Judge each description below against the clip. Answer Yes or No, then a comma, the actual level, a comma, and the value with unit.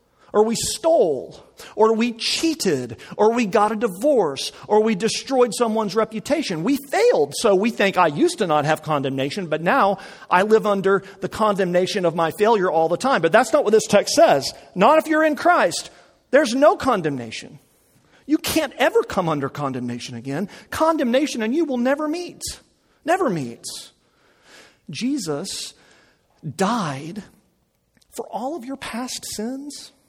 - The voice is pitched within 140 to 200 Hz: No, high, 220 Hz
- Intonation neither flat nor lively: No, wide, 7.4 semitones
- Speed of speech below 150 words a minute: No, average, 155 wpm